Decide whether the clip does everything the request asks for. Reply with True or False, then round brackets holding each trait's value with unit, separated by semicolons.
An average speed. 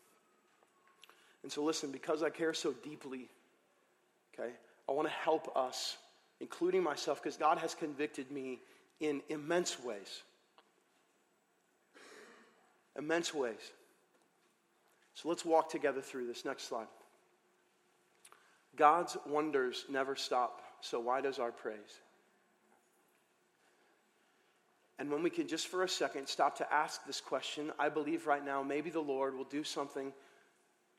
False (125 wpm)